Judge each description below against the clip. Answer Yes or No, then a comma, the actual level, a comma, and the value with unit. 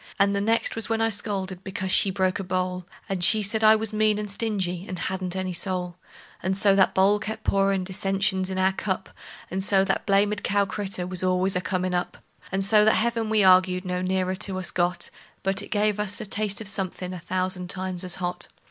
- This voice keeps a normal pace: No, fast, 220 wpm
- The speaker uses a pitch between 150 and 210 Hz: Yes, high, 190 Hz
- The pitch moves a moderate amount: No, narrow, 1.9 semitones